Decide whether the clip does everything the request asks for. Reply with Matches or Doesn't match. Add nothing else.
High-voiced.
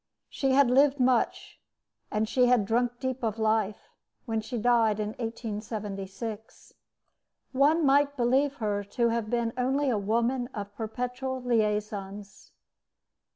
Matches